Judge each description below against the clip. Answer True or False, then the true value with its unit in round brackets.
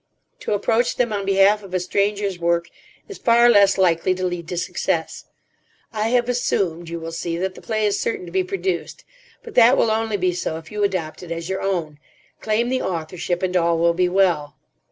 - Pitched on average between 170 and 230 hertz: True (190 Hz)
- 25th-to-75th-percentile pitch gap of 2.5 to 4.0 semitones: False (4.4 semitones)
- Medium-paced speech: False (210 wpm)